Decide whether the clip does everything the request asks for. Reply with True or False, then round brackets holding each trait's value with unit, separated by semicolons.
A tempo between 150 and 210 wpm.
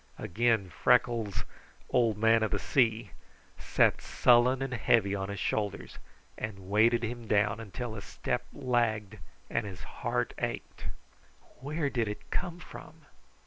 False (140 wpm)